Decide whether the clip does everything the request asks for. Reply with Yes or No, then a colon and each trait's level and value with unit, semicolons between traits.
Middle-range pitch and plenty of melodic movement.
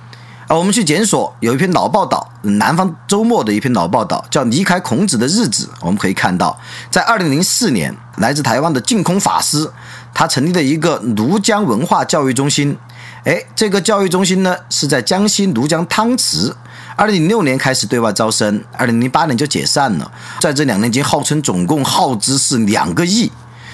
Yes: medium, 160 Hz; wide, 8.2 semitones